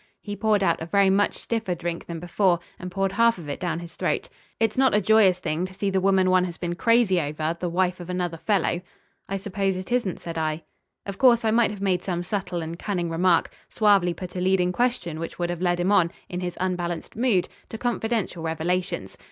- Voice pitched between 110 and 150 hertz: No, medium, 185 Hz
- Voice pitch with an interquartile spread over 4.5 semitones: No, average, 2.7 semitones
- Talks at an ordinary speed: No, fast, 225 wpm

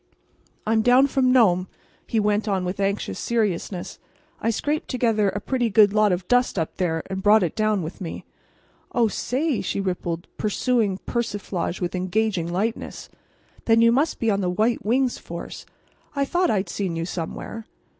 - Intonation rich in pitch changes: No, average, 4.1 semitones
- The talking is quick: No, average, 170 wpm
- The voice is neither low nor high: No, high, 210 Hz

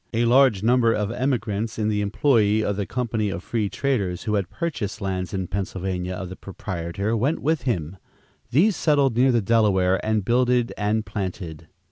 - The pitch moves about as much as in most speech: Yes, average, 4.1 semitones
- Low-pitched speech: Yes, low, 105 Hz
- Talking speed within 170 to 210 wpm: Yes, average, 175 wpm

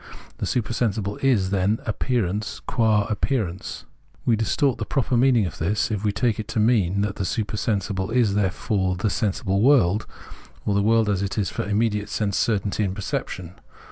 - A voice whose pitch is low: Yes, low, 105 Hz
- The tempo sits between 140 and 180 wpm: Yes, average, 175 wpm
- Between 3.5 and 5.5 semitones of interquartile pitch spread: No, average, 2.7 semitones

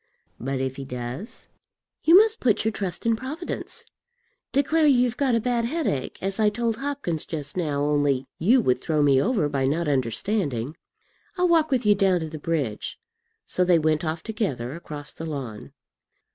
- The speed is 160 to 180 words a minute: Yes, average, 175 wpm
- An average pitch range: No, wide, 8.6 semitones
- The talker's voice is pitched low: No, medium, 170 Hz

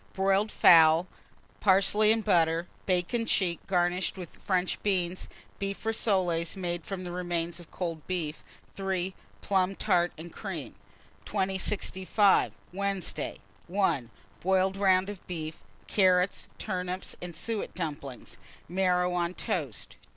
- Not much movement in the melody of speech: Yes, narrow, 2.0 semitones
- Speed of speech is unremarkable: No, slow, 115 wpm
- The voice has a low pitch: No, medium, 185 Hz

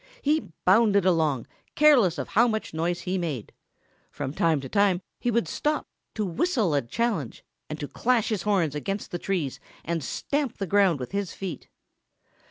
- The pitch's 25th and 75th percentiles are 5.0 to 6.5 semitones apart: Yes, wide, 5.6 semitones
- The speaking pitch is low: No, high, 190 Hz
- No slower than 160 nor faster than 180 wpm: Yes, average, 175 wpm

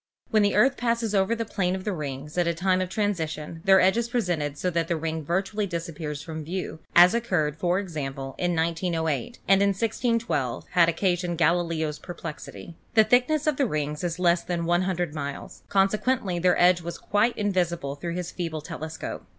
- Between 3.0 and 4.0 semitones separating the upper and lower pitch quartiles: Yes, average, 3.5 semitones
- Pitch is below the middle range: No, medium, 175 Hz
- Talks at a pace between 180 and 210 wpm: Yes, average, 190 wpm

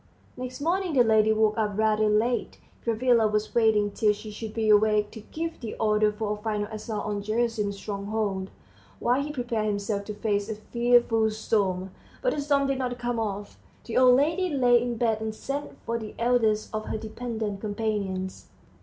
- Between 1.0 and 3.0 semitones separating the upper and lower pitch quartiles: Yes, narrow, 2.5 semitones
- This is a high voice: Yes, high, 220 Hz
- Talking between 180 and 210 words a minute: Yes, average, 185 wpm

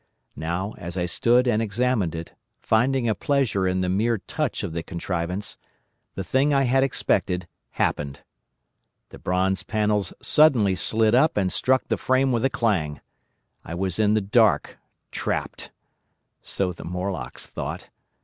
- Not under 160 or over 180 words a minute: No, average, 150 wpm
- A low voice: Yes, low, 105 Hz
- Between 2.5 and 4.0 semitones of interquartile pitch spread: No, average, 5.2 semitones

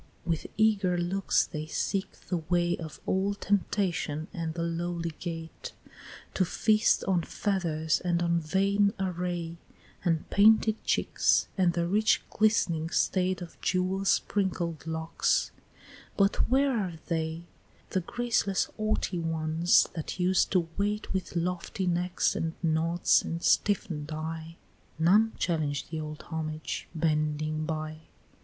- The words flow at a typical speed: No, slow, 130 wpm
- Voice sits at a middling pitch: Yes, medium, 175 Hz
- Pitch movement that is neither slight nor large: Yes, average, 3.1 semitones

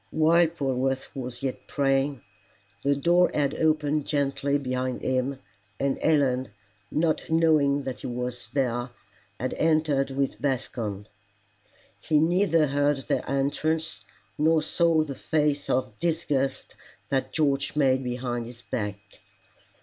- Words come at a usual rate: No, slow, 125 wpm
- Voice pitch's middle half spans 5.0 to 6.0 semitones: No, average, 3.1 semitones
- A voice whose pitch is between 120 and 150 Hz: Yes, medium, 140 Hz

